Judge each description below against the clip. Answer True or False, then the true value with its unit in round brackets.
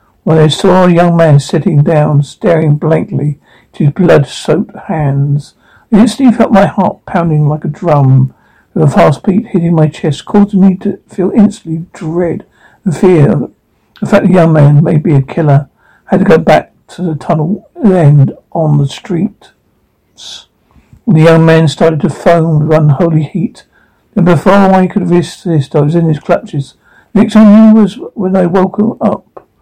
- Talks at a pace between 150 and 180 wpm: True (175 wpm)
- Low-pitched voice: False (170 Hz)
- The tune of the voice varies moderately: True (4.0 semitones)